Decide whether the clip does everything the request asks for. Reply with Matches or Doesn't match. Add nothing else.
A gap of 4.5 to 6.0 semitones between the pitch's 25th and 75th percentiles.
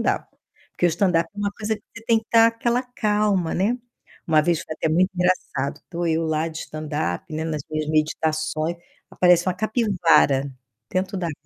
Matches